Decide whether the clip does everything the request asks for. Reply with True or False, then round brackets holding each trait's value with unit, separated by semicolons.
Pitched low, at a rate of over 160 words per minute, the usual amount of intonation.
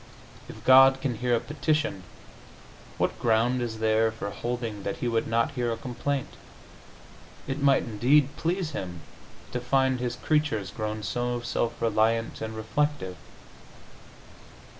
False (120 Hz; 140 wpm; 3.2 semitones)